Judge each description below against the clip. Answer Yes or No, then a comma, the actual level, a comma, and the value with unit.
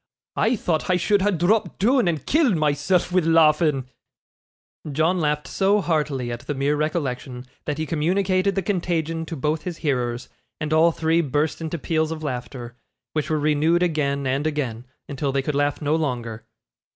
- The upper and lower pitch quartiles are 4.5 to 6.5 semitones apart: No, average, 3.4 semitones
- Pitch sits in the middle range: Yes, medium, 155 Hz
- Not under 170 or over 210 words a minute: Yes, average, 175 wpm